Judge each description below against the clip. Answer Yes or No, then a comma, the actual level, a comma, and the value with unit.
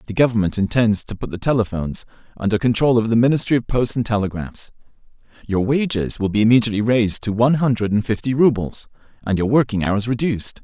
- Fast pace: No, average, 185 wpm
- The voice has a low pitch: Yes, low, 110 Hz